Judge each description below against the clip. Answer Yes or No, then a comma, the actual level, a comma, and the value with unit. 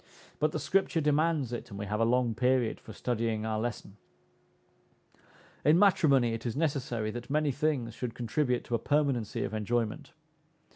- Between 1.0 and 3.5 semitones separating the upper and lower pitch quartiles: No, average, 4.6 semitones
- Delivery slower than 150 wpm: No, average, 165 wpm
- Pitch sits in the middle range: No, low, 125 Hz